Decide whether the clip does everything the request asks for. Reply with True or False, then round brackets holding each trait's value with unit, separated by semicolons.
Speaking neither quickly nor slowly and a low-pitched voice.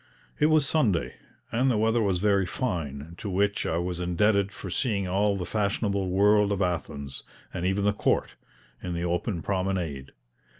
True (170 wpm; 95 Hz)